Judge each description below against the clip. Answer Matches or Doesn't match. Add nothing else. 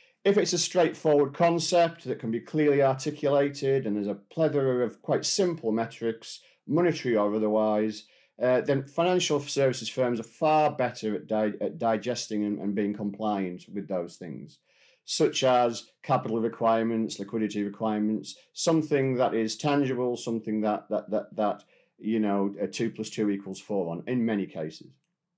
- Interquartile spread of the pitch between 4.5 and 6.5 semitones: Matches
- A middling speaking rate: Matches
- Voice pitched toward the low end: Matches